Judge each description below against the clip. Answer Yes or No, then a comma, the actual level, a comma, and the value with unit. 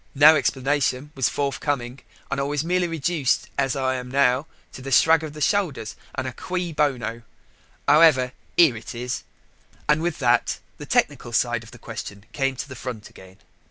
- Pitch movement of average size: Yes, average, 3.4 semitones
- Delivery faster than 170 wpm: Yes, average, 180 wpm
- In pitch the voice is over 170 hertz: No, low, 135 Hz